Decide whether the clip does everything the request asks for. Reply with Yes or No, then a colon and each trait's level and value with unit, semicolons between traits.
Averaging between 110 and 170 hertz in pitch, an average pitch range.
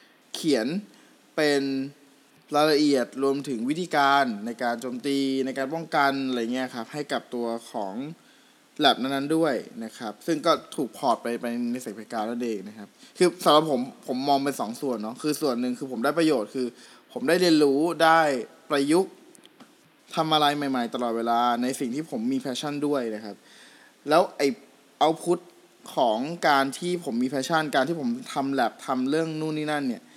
Yes: medium, 140 Hz; average, 4.5 semitones